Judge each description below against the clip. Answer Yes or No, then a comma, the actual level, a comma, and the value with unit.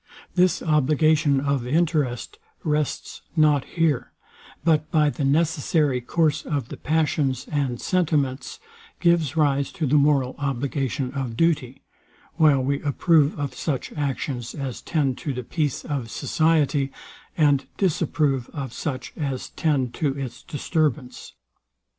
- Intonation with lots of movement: No, average, 2.7 semitones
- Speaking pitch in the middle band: Yes, medium, 145 Hz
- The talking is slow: Yes, slow, 130 wpm